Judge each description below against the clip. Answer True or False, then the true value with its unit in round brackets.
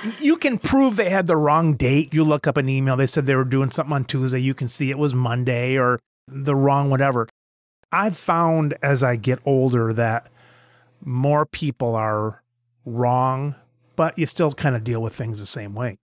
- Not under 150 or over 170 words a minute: False (200 wpm)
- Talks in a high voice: False (135 Hz)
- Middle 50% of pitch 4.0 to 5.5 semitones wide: False (3.4 semitones)